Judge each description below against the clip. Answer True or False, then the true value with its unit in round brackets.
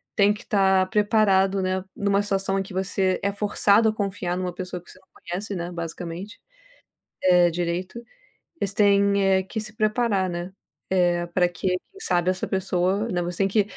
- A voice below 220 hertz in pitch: True (190 Hz)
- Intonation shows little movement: True (2.1 semitones)